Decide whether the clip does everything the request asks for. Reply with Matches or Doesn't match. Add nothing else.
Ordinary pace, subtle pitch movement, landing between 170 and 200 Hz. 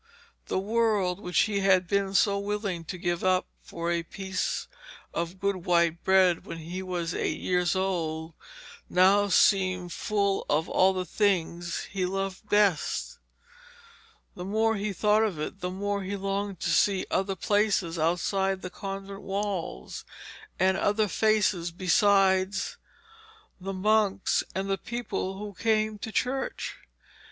Matches